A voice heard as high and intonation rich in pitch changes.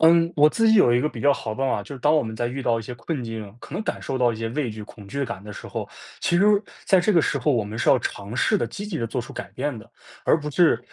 No: low, 130 Hz; wide, 5.8 semitones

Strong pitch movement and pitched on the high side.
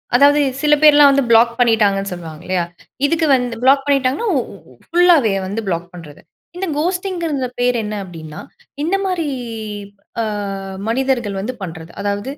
Yes: wide, 7.1 semitones; high, 245 Hz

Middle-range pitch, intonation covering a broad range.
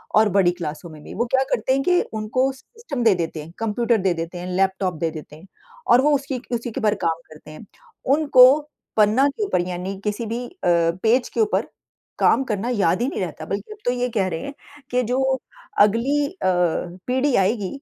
No: high, 215 Hz; wide, 6.0 semitones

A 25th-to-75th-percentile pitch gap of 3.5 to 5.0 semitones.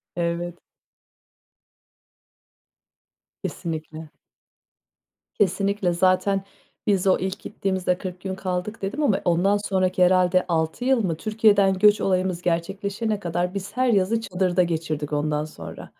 No: narrow, 2.5 semitones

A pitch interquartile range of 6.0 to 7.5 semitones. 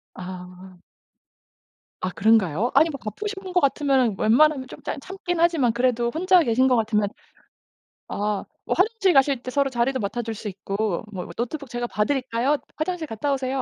No: wide, 5.4 semitones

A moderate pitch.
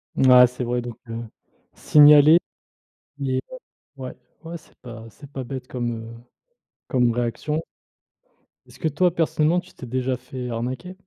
No: low, 130 Hz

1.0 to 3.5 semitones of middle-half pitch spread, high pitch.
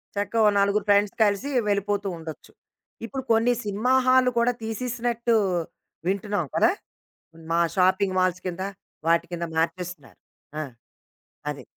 No: average, 3.9 semitones; high, 200 Hz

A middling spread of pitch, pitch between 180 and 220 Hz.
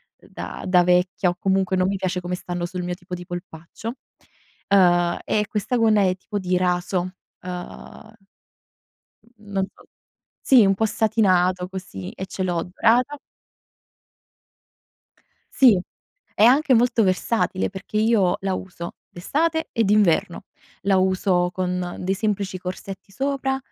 Yes: average, 3.1 semitones; high, 190 Hz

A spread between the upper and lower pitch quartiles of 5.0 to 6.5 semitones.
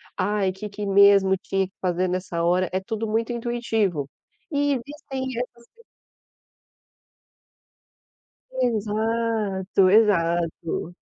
No: average, 3.8 semitones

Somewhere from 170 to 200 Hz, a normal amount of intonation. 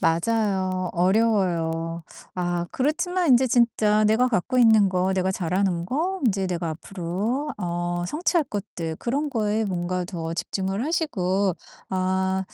Yes: high, 190 Hz; average, 4.7 semitones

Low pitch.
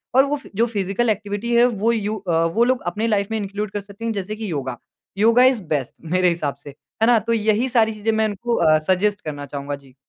No: high, 210 Hz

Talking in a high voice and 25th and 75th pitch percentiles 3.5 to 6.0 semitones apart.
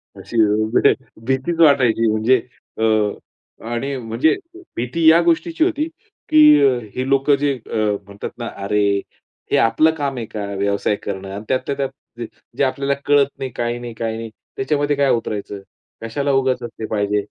No: low, 125 Hz; average, 4.3 semitones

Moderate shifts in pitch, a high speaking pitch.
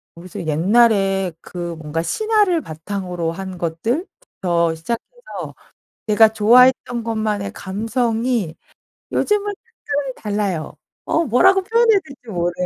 No: wide, 6.8 semitones; high, 215 Hz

